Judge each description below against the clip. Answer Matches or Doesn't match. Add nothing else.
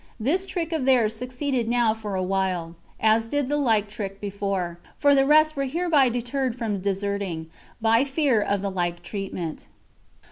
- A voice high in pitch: Matches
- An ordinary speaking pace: Matches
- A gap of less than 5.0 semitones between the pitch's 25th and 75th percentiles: Doesn't match